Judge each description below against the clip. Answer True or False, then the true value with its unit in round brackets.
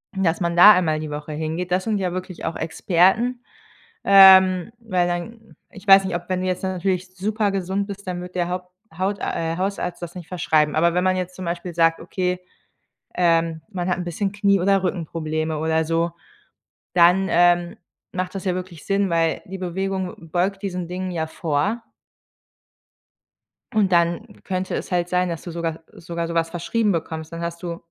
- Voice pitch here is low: False (180 Hz)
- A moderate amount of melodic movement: False (2.2 semitones)